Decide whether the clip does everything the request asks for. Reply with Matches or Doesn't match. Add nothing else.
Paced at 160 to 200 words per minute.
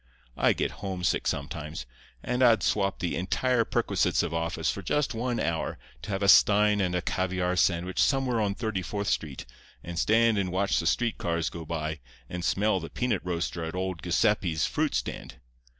Matches